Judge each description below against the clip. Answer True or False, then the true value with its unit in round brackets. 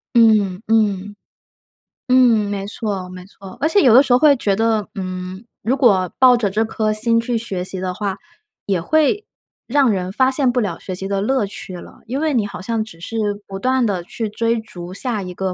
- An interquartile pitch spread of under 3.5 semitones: False (4.2 semitones)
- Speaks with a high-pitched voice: True (215 Hz)